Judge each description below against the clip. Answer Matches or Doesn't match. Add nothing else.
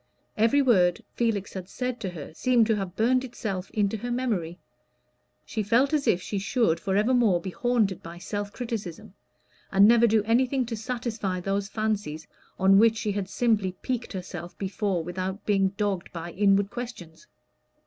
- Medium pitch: Doesn't match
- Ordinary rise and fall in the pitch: Matches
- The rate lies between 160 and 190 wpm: Matches